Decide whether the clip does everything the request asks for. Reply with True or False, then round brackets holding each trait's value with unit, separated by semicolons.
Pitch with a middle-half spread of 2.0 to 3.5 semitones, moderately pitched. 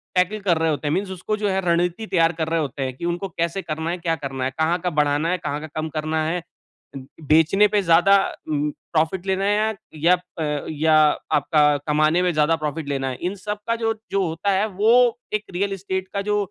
False (4.0 semitones; 170 Hz)